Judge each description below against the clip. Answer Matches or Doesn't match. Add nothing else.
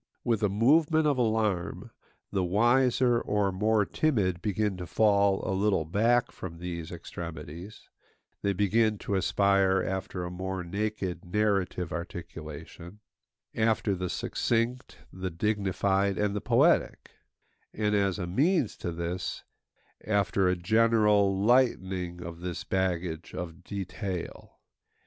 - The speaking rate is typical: Doesn't match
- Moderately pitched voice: Doesn't match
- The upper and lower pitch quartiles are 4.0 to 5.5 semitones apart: Doesn't match